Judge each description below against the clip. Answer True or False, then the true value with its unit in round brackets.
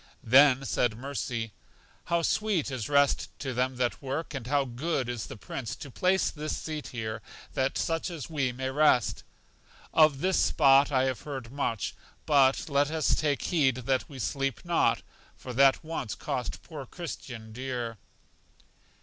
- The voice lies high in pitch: False (135 Hz)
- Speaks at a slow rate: False (160 wpm)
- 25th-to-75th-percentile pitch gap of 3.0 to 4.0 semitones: True (3.3 semitones)